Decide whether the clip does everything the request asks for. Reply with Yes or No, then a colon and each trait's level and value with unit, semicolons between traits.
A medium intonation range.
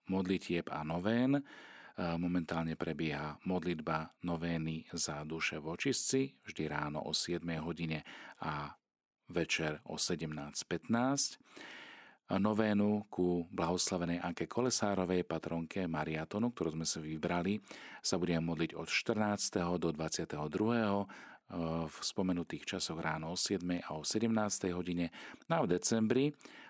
Yes: average, 3.7 semitones